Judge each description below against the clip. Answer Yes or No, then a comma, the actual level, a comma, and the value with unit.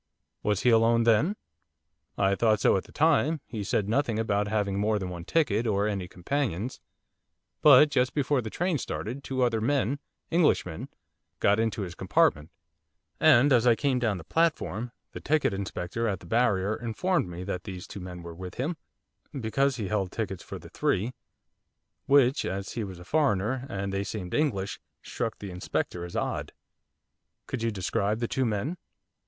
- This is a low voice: Yes, low, 110 Hz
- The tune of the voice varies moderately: Yes, average, 5.0 semitones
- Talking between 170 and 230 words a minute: Yes, average, 180 wpm